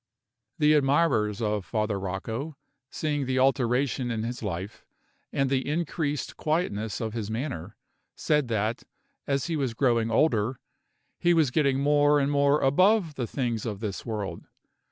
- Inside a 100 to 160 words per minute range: Yes, average, 150 wpm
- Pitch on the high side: No, low, 130 Hz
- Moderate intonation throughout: Yes, average, 4.9 semitones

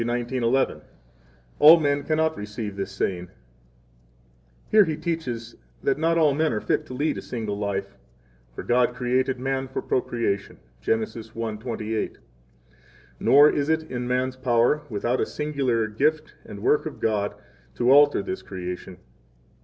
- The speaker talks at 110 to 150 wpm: Yes, average, 145 wpm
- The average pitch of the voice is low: Yes, low, 125 Hz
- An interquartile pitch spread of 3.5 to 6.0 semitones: Yes, average, 4.9 semitones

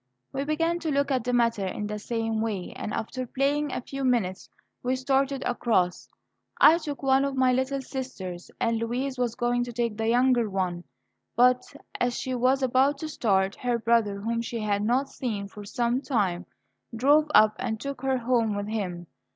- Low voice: No, high, 245 Hz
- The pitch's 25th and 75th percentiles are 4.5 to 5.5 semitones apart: No, average, 3.7 semitones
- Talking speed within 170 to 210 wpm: Yes, average, 190 wpm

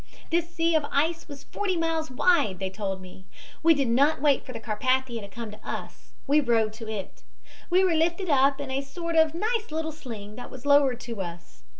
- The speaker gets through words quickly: Yes, fast, 215 wpm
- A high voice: Yes, very high, 275 Hz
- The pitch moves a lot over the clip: Yes, wide, 6.5 semitones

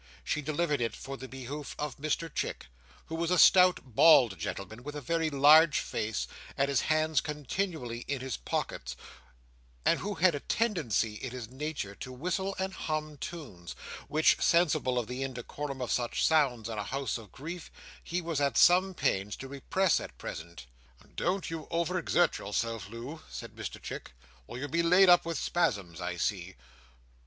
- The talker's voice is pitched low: No, medium, 145 Hz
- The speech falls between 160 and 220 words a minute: Yes, average, 175 wpm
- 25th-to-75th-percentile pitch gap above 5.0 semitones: Yes, wide, 5.4 semitones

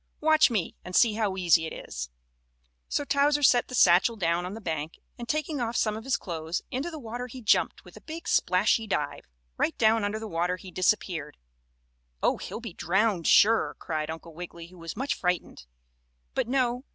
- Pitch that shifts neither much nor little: No, wide, 6.0 semitones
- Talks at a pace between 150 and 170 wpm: No, average, 195 wpm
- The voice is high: Yes, high, 210 Hz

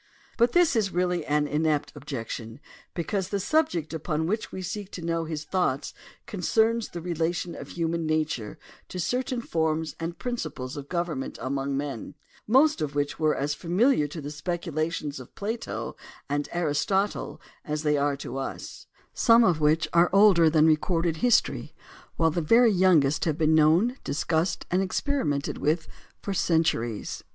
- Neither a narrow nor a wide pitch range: Yes, average, 3.9 semitones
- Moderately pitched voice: Yes, medium, 165 Hz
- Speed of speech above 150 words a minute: Yes, average, 160 wpm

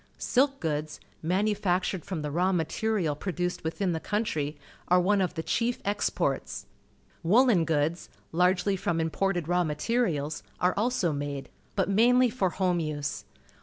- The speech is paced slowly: No, average, 150 wpm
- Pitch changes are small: No, average, 4.2 semitones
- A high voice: No, medium, 180 Hz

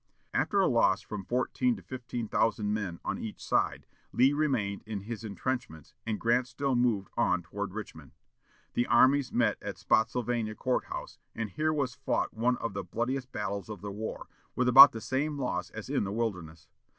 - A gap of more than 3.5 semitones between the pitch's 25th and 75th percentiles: Yes, average, 4.0 semitones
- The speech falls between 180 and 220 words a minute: Yes, average, 185 wpm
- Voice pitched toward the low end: Yes, low, 115 Hz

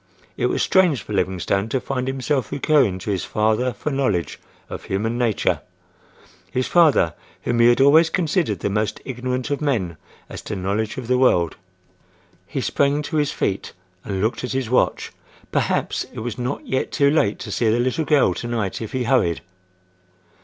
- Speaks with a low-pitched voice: Yes, low, 125 Hz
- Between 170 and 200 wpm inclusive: Yes, average, 180 wpm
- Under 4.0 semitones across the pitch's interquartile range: No, average, 4.7 semitones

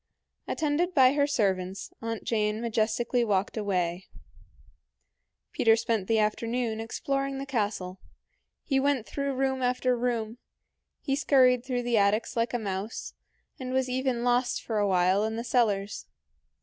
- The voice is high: Yes, high, 235 Hz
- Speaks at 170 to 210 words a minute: No, average, 145 wpm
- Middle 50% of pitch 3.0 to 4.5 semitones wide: Yes, average, 3.5 semitones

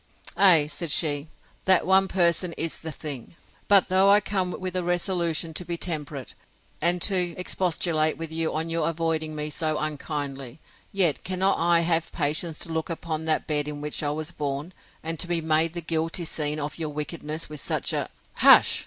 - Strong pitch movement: No, narrow, 2.4 semitones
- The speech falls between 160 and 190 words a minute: Yes, average, 185 wpm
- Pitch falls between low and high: Yes, medium, 165 Hz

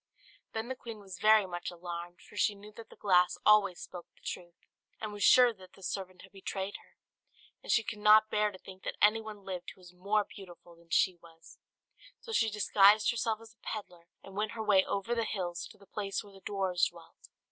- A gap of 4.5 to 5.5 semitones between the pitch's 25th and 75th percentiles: No, average, 2.9 semitones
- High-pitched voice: Yes, high, 200 Hz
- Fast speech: Yes, fast, 220 wpm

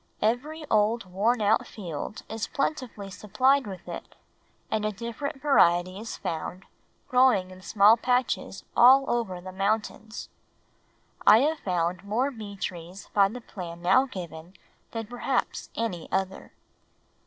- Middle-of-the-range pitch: No, high, 210 Hz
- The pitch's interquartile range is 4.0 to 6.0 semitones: Yes, average, 4.6 semitones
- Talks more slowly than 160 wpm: Yes, slow, 135 wpm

